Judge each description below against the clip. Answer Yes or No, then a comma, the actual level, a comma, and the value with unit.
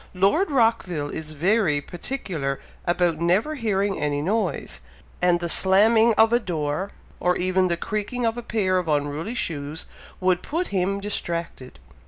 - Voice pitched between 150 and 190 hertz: Yes, medium, 185 Hz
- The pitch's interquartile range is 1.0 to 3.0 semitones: No, average, 5.1 semitones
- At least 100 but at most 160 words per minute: Yes, average, 150 wpm